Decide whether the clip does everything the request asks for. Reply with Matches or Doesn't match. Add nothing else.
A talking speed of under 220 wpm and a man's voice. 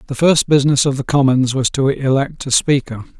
Matches